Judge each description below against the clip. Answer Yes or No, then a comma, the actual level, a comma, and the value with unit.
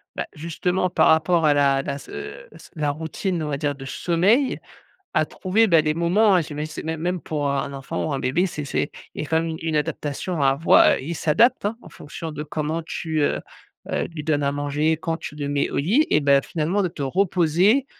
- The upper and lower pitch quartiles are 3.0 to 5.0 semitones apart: Yes, average, 3.3 semitones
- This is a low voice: No, medium, 160 Hz